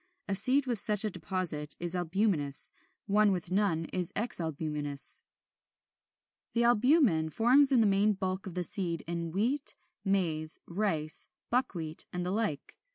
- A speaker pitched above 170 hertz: Yes, medium, 185 Hz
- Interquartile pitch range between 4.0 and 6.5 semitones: Yes, average, 4.6 semitones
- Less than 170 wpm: Yes, average, 145 wpm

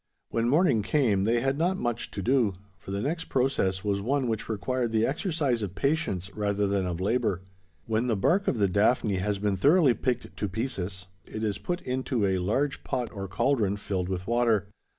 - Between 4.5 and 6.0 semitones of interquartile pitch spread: Yes, average, 4.8 semitones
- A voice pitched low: Yes, low, 110 Hz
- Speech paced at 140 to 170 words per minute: No, average, 195 wpm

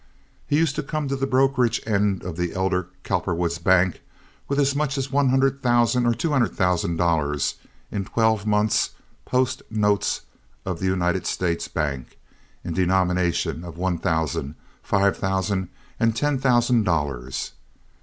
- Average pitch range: No, wide, 6.5 semitones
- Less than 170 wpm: Yes, average, 150 wpm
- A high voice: No, low, 100 Hz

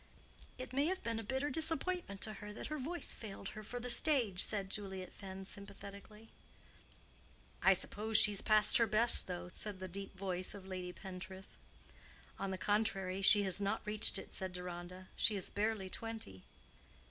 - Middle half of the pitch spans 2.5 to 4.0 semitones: Yes, average, 2.9 semitones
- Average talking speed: Yes, average, 170 wpm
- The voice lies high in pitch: Yes, high, 205 Hz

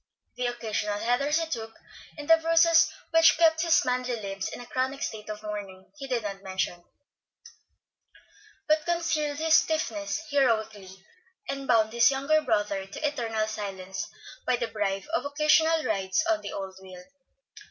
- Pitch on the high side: Yes, high, 245 Hz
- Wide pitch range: Yes, wide, 6.8 semitones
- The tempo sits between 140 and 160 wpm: Yes, average, 155 wpm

